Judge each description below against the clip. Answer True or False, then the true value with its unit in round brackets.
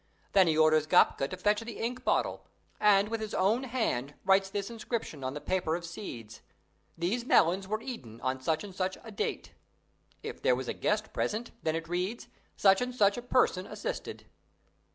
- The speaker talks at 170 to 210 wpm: True (190 wpm)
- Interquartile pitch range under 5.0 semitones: False (5.6 semitones)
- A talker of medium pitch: False (195 Hz)